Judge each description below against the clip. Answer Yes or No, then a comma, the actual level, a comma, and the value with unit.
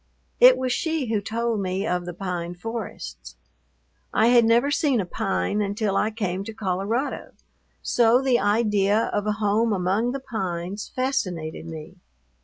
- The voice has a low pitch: No, high, 210 Hz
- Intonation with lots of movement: No, average, 4.0 semitones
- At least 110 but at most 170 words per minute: Yes, average, 155 wpm